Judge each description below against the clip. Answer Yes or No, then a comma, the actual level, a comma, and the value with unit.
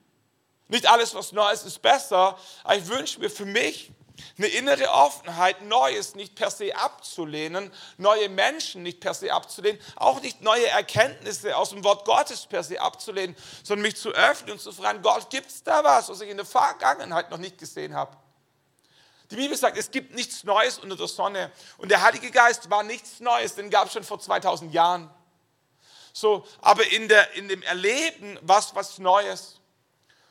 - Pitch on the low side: No, high, 205 Hz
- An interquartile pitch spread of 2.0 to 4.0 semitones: Yes, average, 3.7 semitones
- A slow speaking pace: No, average, 180 wpm